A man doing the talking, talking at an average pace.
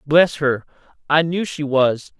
Yes: male; average, 165 wpm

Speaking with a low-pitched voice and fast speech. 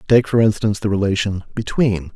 No: low, 105 Hz; average, 165 wpm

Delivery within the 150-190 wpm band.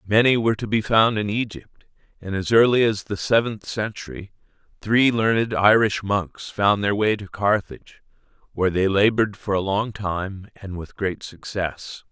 Yes: average, 170 wpm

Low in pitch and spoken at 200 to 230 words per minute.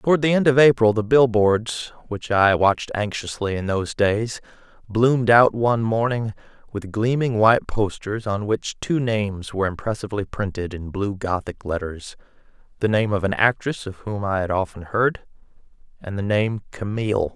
No: low, 105 Hz; average, 165 wpm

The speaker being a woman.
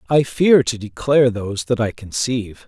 No: male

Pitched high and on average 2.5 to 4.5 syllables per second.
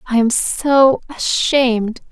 Yes: very high, 250 Hz; 3.4 syllables/s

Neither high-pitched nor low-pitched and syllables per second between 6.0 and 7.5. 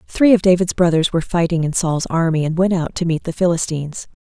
Yes: medium, 170 Hz; 6.1 syllables/s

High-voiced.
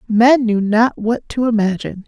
Yes: high, 225 Hz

